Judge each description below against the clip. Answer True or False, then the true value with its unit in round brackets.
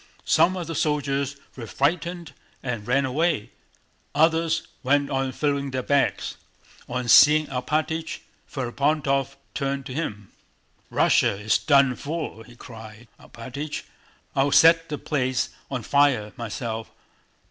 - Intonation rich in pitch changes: False (3.3 semitones)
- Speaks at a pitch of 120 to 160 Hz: True (140 Hz)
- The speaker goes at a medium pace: False (125 wpm)